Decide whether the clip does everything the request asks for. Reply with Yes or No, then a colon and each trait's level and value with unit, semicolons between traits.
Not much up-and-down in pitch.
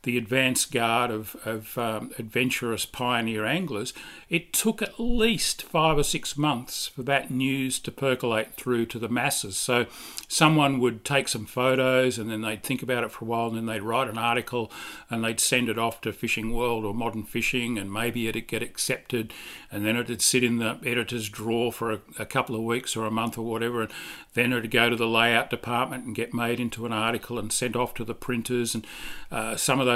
Yes: narrow, 1.9 semitones